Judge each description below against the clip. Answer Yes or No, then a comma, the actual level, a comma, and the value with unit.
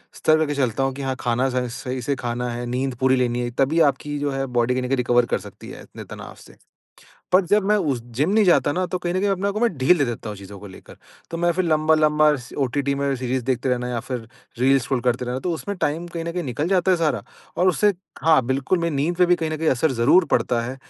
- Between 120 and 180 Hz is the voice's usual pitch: Yes, low, 135 Hz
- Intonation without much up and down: No, average, 4.9 semitones